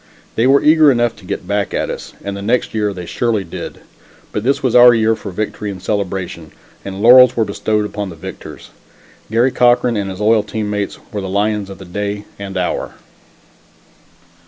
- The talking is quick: No, average, 195 wpm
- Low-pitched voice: Yes, low, 105 Hz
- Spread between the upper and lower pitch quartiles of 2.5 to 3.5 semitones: Yes, average, 2.9 semitones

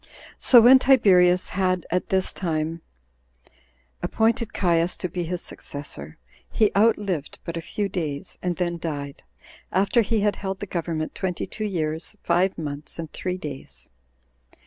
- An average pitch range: Yes, average, 3.6 semitones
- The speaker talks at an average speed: Yes, average, 150 wpm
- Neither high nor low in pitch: Yes, medium, 180 Hz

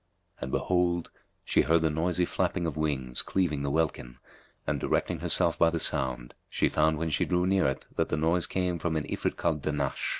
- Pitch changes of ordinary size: Yes, average, 3.5 semitones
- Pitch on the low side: Yes, very low, 80 Hz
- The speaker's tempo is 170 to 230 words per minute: Yes, average, 200 wpm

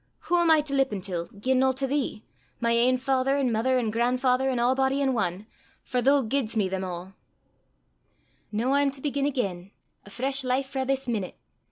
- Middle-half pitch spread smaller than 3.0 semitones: No, average, 3.7 semitones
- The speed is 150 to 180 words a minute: No, average, 195 wpm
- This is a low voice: No, very high, 255 Hz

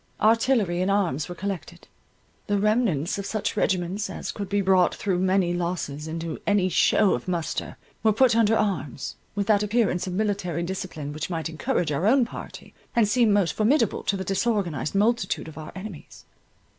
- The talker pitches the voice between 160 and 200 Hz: Yes, high, 190 Hz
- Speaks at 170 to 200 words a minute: Yes, average, 175 wpm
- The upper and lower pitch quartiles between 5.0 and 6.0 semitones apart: No, average, 3.7 semitones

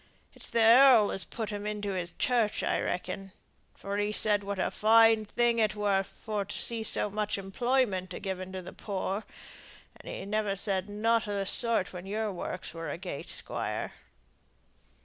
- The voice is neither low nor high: No, high, 205 Hz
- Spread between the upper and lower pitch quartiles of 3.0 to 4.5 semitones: No, narrow, 2.4 semitones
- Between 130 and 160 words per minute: No, average, 180 wpm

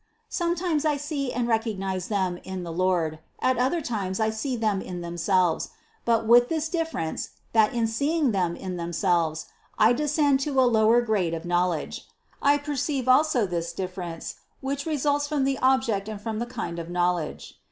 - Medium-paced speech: Yes, average, 175 wpm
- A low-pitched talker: No, high, 220 Hz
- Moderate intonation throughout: No, wide, 7.3 semitones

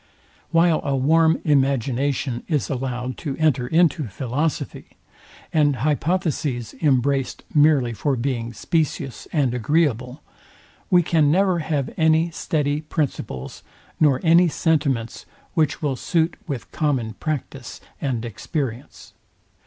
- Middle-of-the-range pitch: Yes, medium, 145 Hz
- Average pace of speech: No, slow, 115 wpm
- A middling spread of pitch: Yes, average, 3.9 semitones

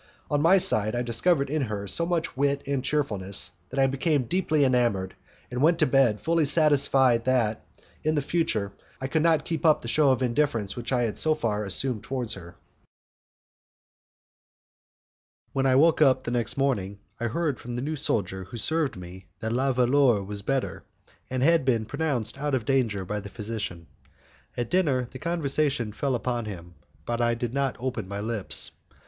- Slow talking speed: No, average, 185 wpm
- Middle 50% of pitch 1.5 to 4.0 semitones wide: No, average, 4.7 semitones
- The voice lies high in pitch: No, low, 130 Hz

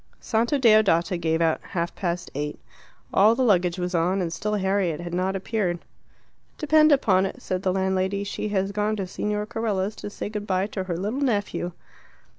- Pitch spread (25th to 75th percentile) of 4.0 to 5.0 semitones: No, average, 2.9 semitones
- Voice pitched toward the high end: Yes, high, 195 Hz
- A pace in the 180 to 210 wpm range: Yes, average, 185 wpm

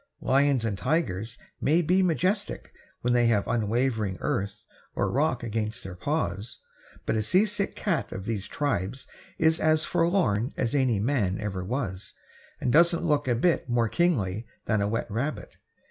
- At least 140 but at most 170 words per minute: Yes, average, 160 wpm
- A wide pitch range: Yes, wide, 7.0 semitones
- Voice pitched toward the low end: Yes, low, 120 Hz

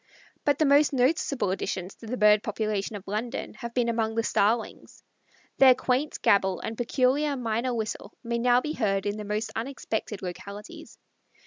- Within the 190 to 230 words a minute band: No, average, 165 wpm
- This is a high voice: Yes, high, 230 Hz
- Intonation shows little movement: No, average, 3.4 semitones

